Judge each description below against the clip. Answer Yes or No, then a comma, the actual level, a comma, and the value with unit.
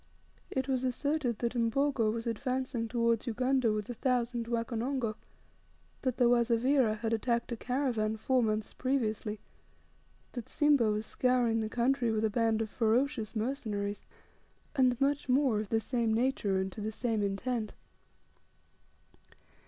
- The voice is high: Yes, high, 235 Hz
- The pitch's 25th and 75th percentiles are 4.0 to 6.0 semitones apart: No, average, 2.8 semitones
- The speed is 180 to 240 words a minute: No, average, 145 wpm